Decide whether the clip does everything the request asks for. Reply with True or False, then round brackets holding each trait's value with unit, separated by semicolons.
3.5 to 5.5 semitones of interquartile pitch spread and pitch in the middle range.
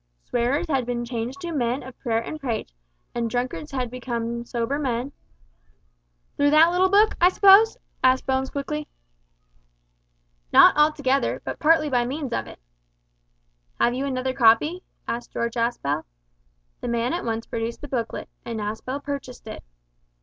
False (3.9 semitones; 255 Hz)